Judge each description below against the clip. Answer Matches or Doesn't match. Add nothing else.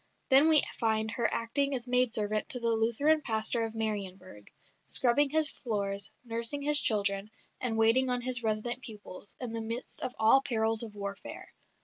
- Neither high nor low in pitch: Doesn't match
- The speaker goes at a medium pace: Matches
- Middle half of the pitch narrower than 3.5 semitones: Matches